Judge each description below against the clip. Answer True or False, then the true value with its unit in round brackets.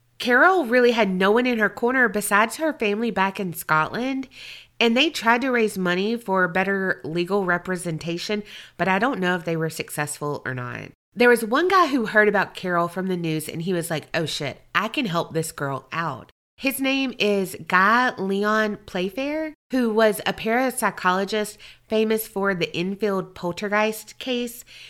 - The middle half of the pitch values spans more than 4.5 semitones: True (5.2 semitones)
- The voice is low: False (200 Hz)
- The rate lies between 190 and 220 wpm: False (175 wpm)